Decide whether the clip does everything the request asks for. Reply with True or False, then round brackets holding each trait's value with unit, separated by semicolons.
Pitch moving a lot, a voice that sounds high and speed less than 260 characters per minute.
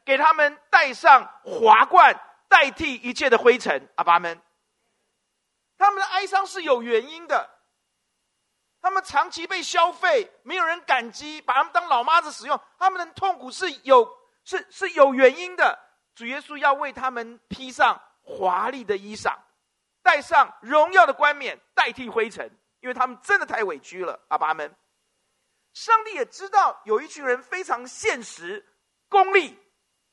True (7.0 semitones; 320 Hz; 225 characters per minute)